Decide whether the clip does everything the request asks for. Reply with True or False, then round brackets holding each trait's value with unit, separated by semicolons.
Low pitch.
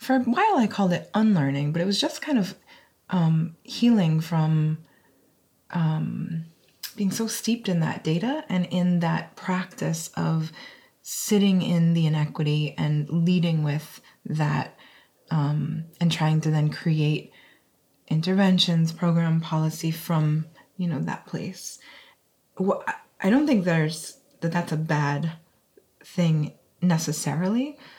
False (165 Hz)